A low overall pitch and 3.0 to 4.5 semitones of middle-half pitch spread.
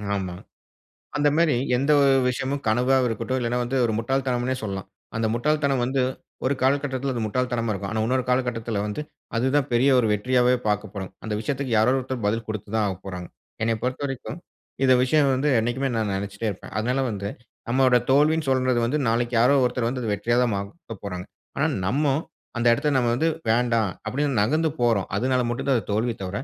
Yes: low, 120 Hz; average, 3.3 semitones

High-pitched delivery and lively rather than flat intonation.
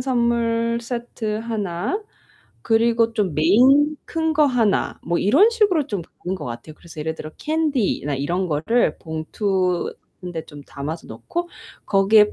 Yes: high, 215 Hz; wide, 6.4 semitones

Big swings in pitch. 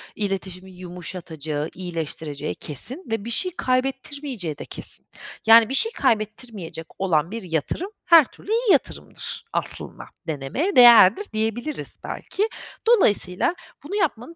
Yes: wide, 8.3 semitones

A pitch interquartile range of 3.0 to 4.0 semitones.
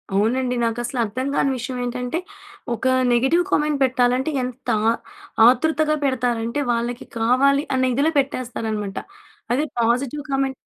No: narrow, 2.5 semitones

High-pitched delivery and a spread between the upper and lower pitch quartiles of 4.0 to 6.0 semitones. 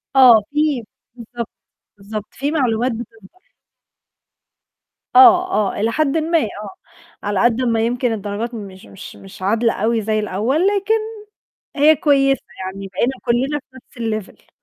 Yes: high, 235 Hz; average, 4.3 semitones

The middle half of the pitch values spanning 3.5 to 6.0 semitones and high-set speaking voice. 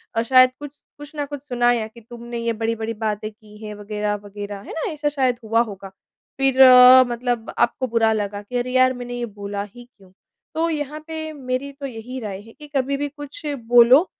Yes: average, 3.8 semitones; high, 240 Hz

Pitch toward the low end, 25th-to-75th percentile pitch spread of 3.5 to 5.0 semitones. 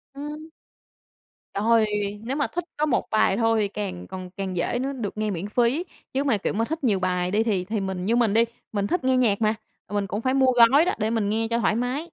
No: high, 225 Hz; average, 4.2 semitones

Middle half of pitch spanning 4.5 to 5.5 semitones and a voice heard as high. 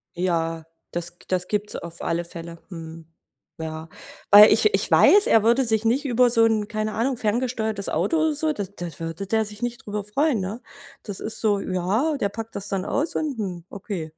Yes: average, 4.8 semitones; high, 210 Hz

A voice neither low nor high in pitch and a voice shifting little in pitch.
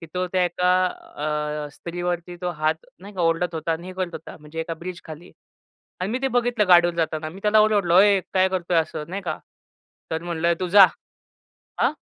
Yes: medium, 175 Hz; narrow, 2.2 semitones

